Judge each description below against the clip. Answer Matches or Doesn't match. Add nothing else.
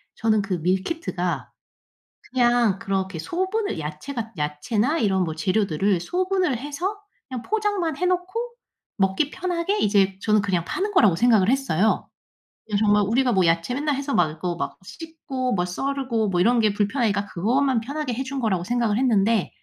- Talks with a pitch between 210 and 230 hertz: Matches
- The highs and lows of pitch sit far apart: Matches